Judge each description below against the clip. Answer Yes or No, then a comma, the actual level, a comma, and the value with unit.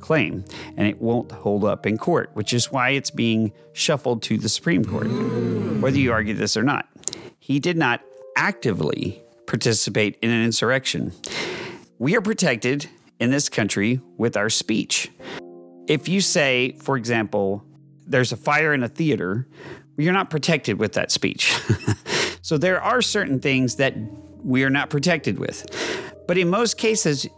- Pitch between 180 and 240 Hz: No, low, 130 Hz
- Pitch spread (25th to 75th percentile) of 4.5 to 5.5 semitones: Yes, average, 5.1 semitones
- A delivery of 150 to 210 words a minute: Yes, average, 160 wpm